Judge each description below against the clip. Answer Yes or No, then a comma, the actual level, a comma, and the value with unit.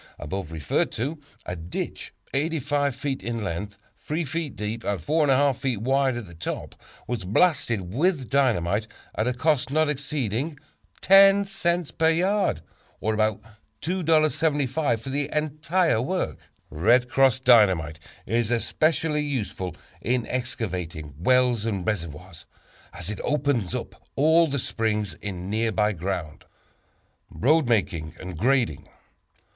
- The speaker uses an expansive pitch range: Yes, wide, 6.8 semitones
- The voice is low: Yes, low, 120 Hz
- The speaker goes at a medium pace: No, slow, 130 wpm